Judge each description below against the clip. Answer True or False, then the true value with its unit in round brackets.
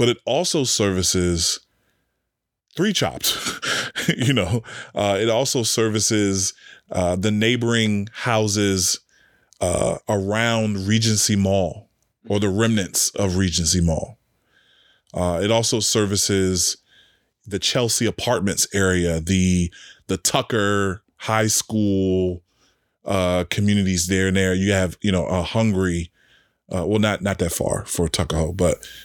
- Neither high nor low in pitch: False (100 Hz)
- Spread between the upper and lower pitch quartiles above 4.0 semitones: False (3.1 semitones)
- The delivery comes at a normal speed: False (120 wpm)